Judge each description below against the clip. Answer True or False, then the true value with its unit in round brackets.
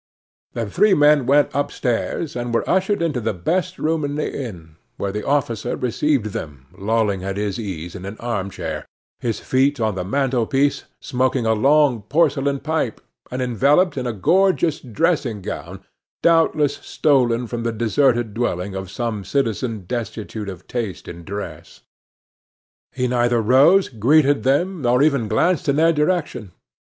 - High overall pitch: False (125 Hz)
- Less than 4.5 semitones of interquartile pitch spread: False (5.3 semitones)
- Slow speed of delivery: False (155 wpm)